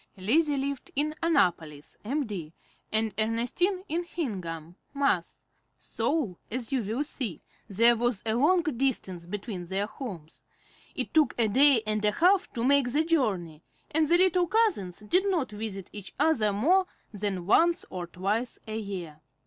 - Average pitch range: No, wide, 7.4 semitones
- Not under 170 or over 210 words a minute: No, average, 155 wpm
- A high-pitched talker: Yes, high, 230 Hz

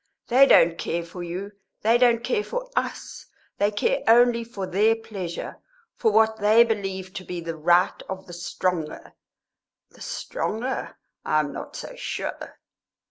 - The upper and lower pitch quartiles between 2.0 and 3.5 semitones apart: No, average, 4.8 semitones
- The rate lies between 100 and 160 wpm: Yes, average, 155 wpm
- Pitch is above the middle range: Yes, high, 205 Hz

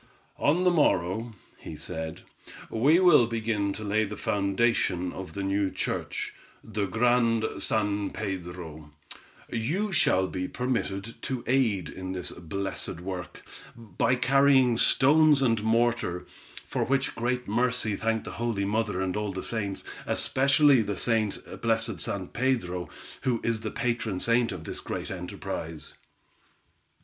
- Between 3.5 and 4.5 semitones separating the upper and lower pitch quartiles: Yes, average, 4.2 semitones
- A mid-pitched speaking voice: No, low, 110 Hz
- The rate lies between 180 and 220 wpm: No, slow, 135 wpm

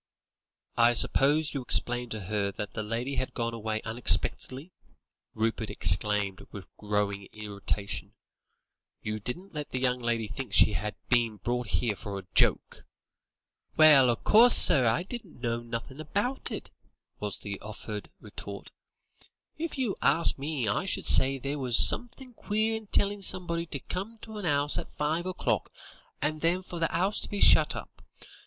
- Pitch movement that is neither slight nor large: No, wide, 7.6 semitones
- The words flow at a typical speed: Yes, average, 165 wpm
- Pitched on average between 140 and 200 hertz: No, low, 130 Hz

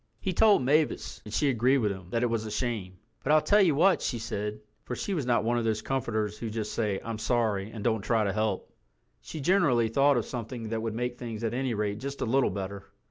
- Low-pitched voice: Yes, low, 115 Hz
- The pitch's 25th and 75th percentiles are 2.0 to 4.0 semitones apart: Yes, average, 3.7 semitones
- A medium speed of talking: No, fast, 245 wpm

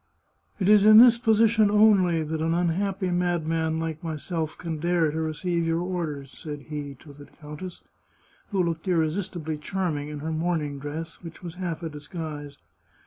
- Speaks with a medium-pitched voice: Yes, medium, 165 Hz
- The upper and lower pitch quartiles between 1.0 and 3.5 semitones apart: Yes, average, 2.8 semitones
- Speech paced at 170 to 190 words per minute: Yes, average, 175 wpm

